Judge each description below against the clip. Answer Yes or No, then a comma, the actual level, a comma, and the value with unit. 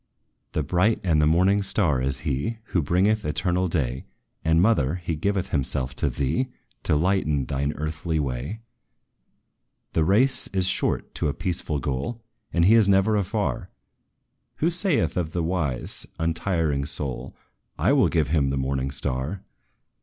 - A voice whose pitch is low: Yes, very low, 80 Hz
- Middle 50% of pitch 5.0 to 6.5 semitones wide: Yes, wide, 5.4 semitones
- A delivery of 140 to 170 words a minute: Yes, average, 155 wpm